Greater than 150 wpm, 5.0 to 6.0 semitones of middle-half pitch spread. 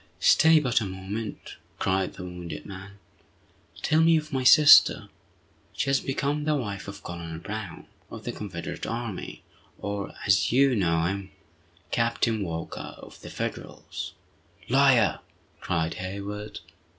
No: slow, 135 wpm; wide, 5.6 semitones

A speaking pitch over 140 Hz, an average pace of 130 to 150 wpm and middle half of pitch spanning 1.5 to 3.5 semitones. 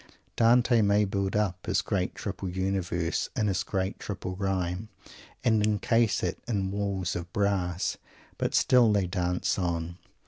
No: very low, 95 Hz; average, 145 wpm; average, 2.7 semitones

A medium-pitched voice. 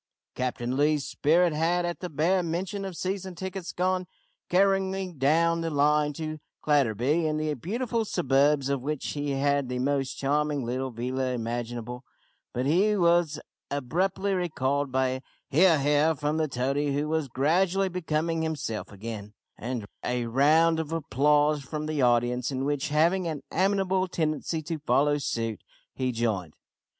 Yes: medium, 150 Hz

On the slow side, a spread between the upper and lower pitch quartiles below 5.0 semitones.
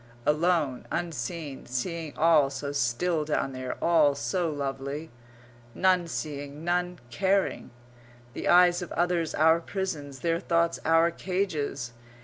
Yes: slow, 125 wpm; average, 3.6 semitones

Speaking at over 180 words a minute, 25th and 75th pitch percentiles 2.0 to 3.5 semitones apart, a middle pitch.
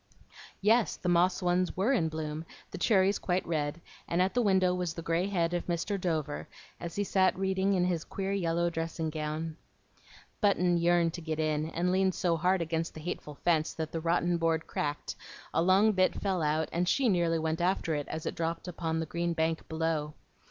Yes: average, 200 wpm; narrow, 2.4 semitones; medium, 170 Hz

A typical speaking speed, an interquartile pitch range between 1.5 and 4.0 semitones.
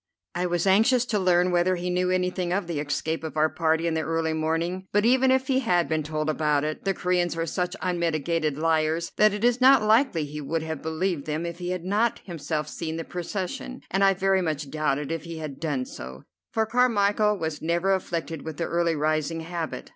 No: fast, 215 wpm; average, 3.2 semitones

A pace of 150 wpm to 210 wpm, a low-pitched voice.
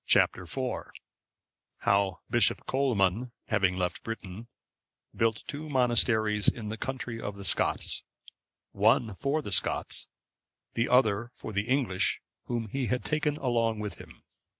No: average, 140 wpm; low, 115 Hz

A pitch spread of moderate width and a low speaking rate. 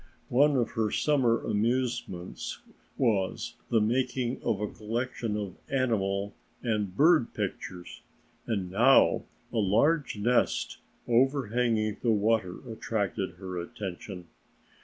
Yes: average, 3.7 semitones; slow, 110 wpm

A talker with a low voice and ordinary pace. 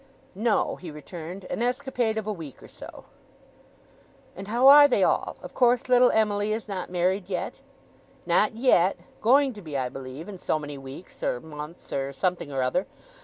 No: high, 190 Hz; average, 180 wpm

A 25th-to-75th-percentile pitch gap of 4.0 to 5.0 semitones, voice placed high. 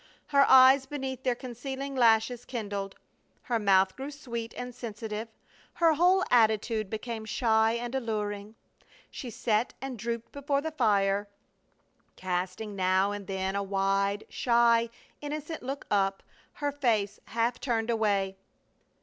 Yes: average, 4.3 semitones; high, 230 Hz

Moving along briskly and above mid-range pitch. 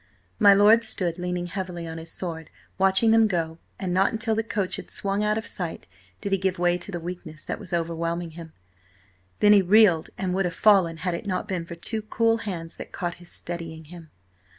No: fast, 215 wpm; medium, 180 Hz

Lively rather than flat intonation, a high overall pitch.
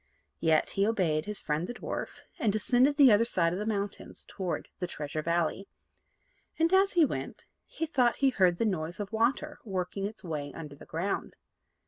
Yes: wide, 6.1 semitones; high, 200 Hz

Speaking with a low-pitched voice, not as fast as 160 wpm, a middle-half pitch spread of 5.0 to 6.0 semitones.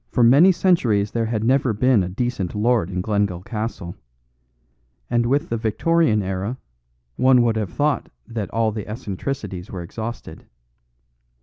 No: low, 115 Hz; average, 140 wpm; average, 3.6 semitones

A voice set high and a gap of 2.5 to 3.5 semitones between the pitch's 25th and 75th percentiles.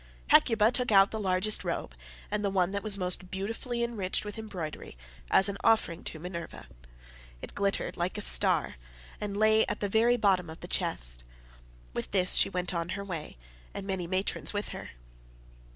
Yes: high, 195 Hz; average, 2.8 semitones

